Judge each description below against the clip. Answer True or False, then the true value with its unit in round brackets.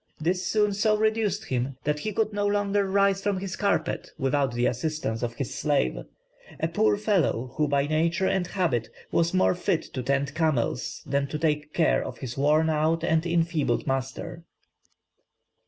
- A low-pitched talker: False (160 Hz)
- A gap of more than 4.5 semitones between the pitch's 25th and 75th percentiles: True (5.5 semitones)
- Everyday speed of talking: True (170 wpm)